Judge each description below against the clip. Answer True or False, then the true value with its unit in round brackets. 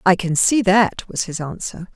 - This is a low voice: False (190 Hz)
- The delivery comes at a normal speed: False (215 wpm)